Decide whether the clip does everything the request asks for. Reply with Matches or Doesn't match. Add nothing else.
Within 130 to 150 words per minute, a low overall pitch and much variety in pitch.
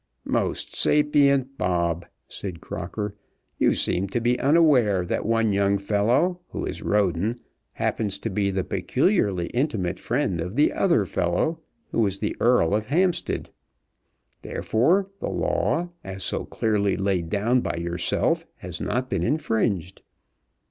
Matches